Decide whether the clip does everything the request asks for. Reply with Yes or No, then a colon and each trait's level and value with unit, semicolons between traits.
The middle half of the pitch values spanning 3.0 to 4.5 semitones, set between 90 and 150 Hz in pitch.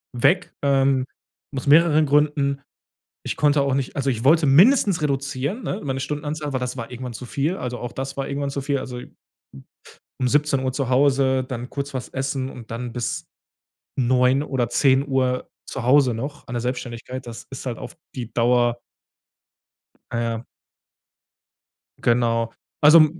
No: narrow, 2.4 semitones; low, 135 Hz